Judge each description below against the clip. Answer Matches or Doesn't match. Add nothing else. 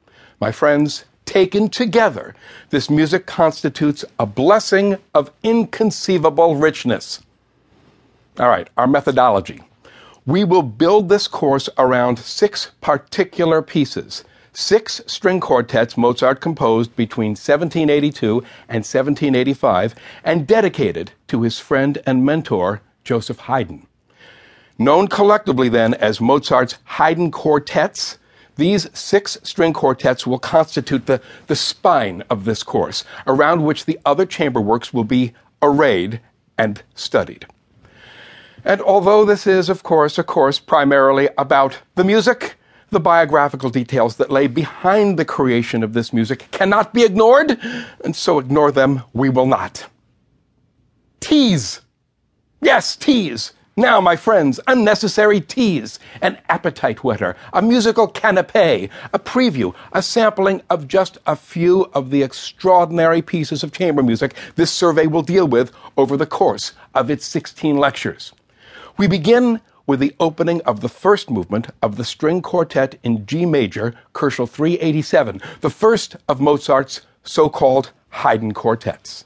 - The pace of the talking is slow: Matches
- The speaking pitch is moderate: Matches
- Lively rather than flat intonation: Matches